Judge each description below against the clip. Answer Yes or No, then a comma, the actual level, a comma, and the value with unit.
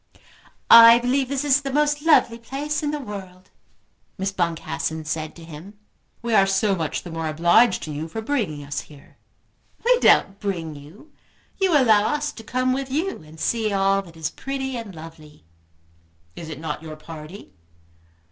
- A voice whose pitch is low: No, high, 195 Hz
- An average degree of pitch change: No, wide, 8.4 semitones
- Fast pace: No, average, 175 wpm